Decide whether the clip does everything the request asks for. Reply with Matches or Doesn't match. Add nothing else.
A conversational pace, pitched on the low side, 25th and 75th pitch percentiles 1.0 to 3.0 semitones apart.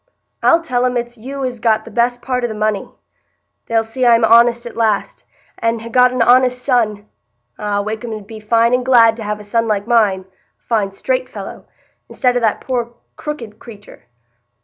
Doesn't match